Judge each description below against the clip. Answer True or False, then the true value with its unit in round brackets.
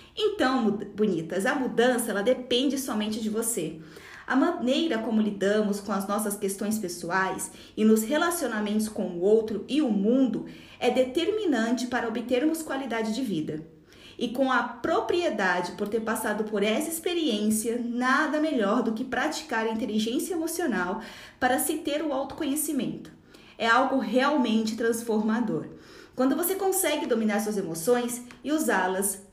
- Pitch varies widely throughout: False (4.2 semitones)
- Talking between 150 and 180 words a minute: False (140 wpm)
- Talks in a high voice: True (235 Hz)